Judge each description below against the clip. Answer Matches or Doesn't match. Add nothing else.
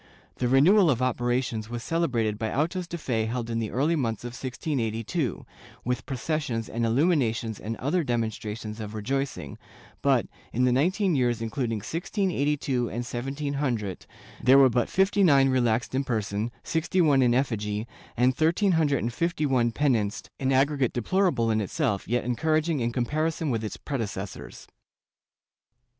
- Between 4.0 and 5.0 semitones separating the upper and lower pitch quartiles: Matches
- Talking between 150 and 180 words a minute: Matches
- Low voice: Matches